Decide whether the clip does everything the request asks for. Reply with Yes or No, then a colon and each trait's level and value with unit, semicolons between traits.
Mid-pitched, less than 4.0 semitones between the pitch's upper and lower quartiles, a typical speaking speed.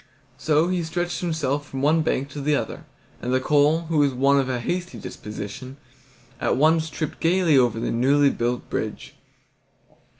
Yes: medium, 145 Hz; average, 3.6 semitones; average, 170 wpm